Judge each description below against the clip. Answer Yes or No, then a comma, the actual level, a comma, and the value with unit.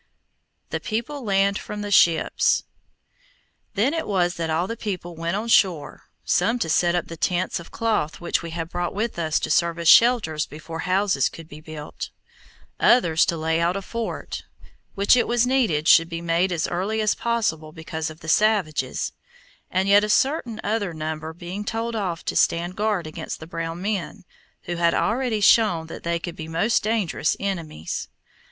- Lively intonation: No, average, 4.5 semitones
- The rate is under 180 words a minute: No, average, 185 wpm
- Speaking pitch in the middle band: Yes, medium, 175 Hz